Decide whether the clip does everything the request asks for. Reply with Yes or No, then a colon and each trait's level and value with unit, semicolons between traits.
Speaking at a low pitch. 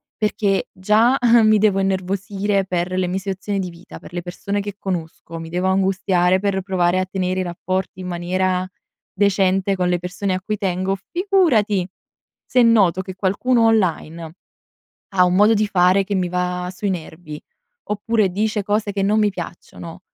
No: high, 190 Hz